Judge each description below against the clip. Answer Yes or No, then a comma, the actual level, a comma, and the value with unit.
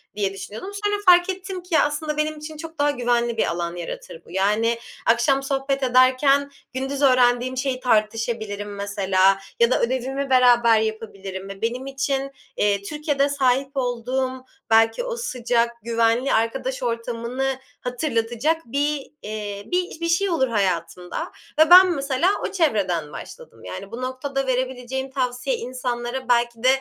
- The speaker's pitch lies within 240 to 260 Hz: Yes, very high, 255 Hz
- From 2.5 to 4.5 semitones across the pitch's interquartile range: Yes, average, 3.6 semitones